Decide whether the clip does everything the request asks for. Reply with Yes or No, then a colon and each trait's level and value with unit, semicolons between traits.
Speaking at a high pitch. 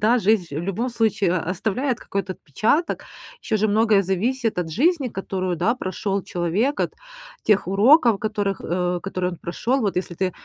Yes: high, 200 Hz